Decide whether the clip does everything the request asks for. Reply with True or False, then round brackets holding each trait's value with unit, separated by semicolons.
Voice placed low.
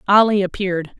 False (195 Hz)